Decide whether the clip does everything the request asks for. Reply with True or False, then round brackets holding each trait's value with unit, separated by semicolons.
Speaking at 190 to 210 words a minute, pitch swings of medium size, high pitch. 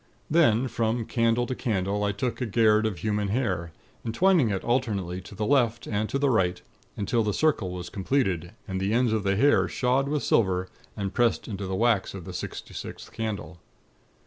False (195 wpm; 4.0 semitones; 110 Hz)